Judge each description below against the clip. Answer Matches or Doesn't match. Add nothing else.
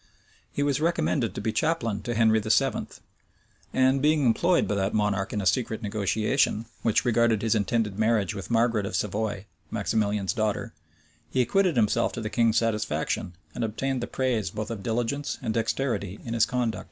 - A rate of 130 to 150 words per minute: Doesn't match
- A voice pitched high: Doesn't match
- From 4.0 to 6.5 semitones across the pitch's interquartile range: Doesn't match